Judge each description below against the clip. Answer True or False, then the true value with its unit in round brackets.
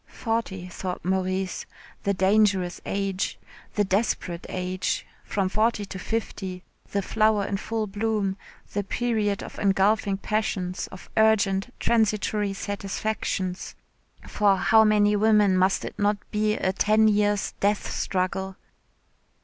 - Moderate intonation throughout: False (2.0 semitones)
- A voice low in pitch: False (200 Hz)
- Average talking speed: False (125 wpm)